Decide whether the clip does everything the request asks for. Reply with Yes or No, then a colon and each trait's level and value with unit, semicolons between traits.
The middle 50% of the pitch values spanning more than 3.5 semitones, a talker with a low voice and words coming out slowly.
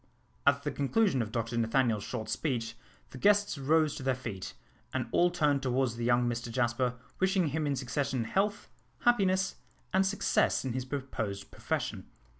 No: average, 5.1 semitones; low, 130 Hz; average, 165 wpm